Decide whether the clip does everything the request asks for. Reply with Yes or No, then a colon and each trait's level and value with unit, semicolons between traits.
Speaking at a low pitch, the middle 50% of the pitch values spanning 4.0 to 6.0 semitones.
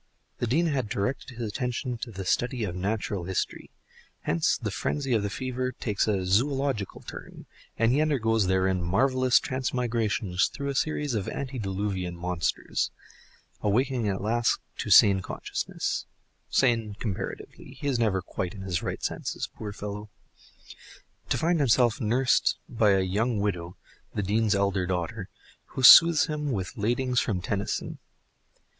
Yes: low, 110 Hz; average, 4.8 semitones